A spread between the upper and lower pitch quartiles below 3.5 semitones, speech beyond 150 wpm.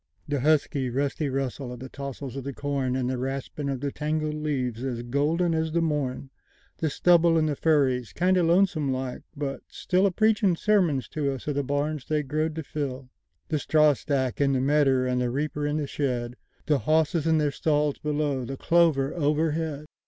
Yes: average, 2.8 semitones; average, 170 wpm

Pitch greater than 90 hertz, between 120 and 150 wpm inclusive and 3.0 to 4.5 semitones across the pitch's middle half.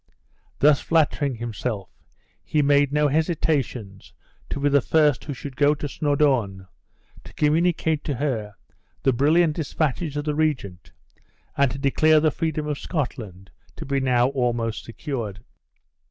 Yes: medium, 140 Hz; average, 140 wpm; average, 3.9 semitones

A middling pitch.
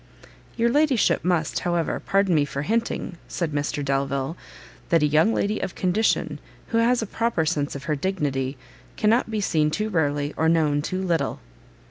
Yes: medium, 165 Hz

